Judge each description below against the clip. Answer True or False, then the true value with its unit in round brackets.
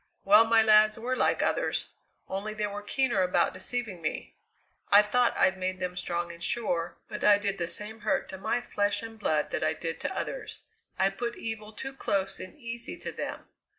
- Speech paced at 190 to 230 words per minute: True (200 wpm)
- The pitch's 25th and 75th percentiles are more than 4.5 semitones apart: False (3.2 semitones)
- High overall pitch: True (210 Hz)